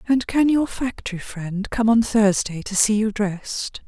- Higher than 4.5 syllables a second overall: No, 4.4 syllables/s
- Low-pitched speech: No, high, 215 Hz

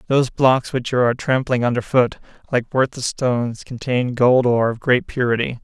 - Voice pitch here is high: No, low, 125 Hz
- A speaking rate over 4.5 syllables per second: Yes, 5.3 syllables/s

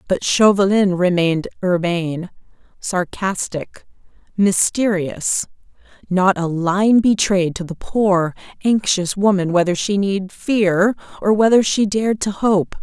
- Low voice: No, high, 190 Hz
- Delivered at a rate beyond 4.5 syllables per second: No, 4.0 syllables/s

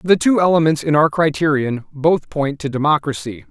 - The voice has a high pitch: No, medium, 150 Hz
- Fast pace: No, average, 170 wpm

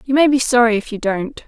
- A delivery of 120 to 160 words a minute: No, fast, 285 wpm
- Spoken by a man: No, female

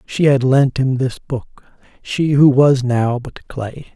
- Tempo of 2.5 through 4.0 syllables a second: Yes, 3.5 syllables/s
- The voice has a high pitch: No, low, 130 Hz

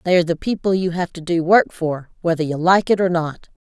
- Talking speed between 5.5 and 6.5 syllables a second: Yes, 5.8 syllables/s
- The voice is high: No, medium, 175 Hz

